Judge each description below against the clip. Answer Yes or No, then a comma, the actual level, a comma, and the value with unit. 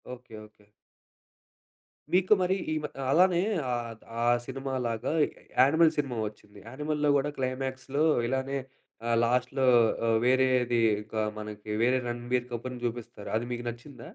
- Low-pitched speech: Yes, low, 125 Hz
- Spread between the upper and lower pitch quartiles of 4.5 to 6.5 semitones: No, narrow, 2.4 semitones